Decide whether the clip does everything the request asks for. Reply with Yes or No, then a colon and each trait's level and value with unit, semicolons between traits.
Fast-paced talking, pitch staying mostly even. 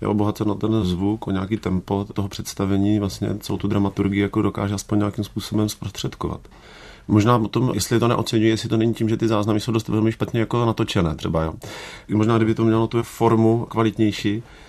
Yes: fast, 195 wpm; narrow, 1.8 semitones